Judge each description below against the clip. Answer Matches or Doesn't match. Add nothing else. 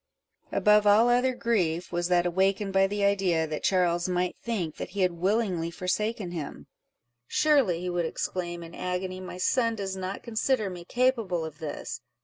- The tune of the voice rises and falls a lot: Doesn't match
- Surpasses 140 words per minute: Matches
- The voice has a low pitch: Doesn't match